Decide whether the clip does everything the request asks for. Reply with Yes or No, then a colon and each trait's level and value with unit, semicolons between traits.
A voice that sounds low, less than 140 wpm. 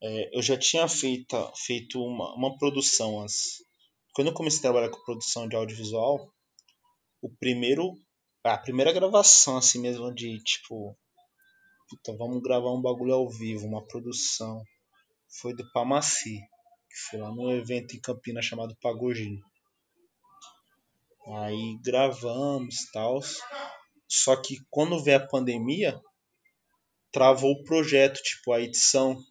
Yes: low, 125 Hz; average, 130 wpm